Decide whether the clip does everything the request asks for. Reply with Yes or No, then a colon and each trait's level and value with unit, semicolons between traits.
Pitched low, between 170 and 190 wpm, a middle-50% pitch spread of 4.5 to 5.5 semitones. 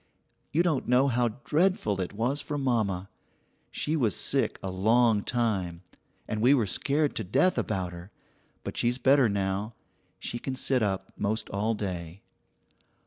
No: low, 110 Hz; average, 155 wpm; average, 5.2 semitones